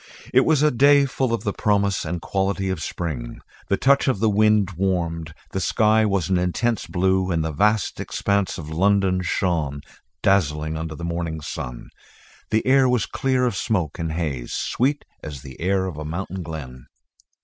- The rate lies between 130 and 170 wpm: No, average, 180 wpm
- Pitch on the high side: No, very low, 95 Hz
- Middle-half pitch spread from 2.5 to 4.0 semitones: No, average, 4.9 semitones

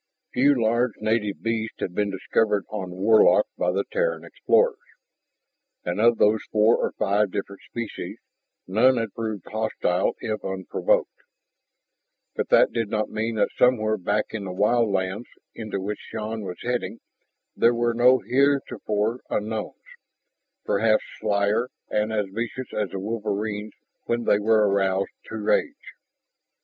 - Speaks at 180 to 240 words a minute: No, average, 140 wpm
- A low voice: Yes, low, 110 Hz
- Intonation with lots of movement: No, narrow, 2.4 semitones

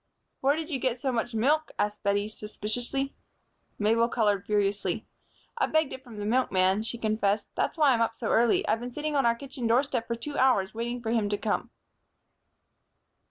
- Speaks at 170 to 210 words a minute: Yes, average, 190 wpm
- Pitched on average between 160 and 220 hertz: No, high, 230 Hz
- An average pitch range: Yes, average, 3.7 semitones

